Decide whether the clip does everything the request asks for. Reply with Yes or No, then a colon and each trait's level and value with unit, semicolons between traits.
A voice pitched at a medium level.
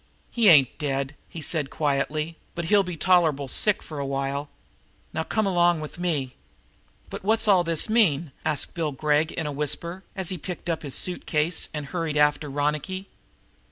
Yes: medium, 160 Hz